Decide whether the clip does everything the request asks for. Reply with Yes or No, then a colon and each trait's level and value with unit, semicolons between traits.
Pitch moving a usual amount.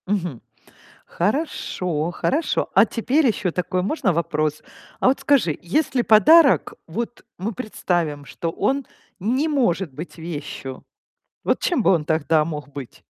No: wide, 7.6 semitones